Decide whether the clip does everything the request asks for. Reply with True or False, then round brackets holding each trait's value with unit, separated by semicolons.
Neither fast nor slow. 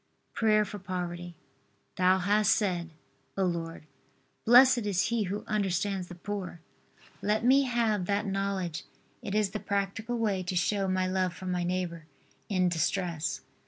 True (150 wpm)